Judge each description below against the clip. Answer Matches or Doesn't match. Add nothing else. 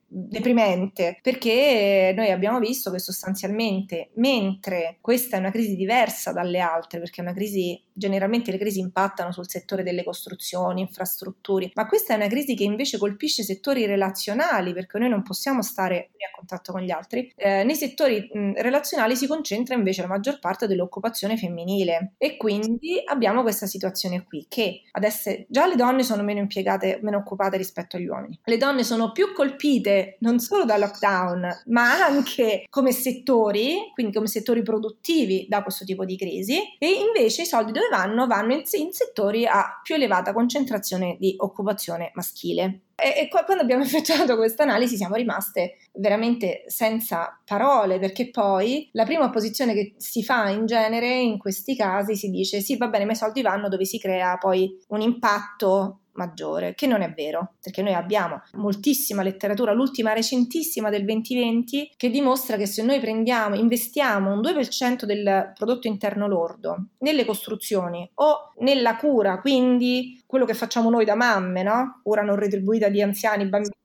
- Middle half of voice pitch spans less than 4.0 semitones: Doesn't match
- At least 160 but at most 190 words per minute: Matches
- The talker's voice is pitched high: Matches